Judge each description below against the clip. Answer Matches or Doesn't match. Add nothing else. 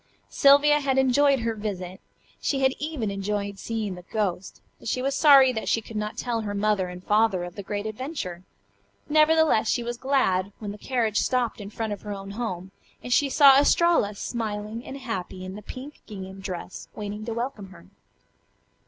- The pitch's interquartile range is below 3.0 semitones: Doesn't match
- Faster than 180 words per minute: Matches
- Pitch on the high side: Matches